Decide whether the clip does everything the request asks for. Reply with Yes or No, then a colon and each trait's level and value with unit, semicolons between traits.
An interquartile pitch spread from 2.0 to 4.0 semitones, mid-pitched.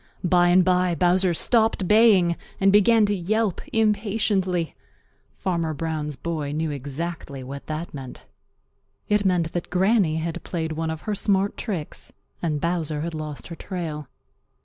Yes: average, 3.7 semitones; medium, 175 Hz